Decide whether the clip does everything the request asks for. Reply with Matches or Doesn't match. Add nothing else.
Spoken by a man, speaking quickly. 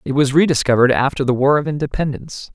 Doesn't match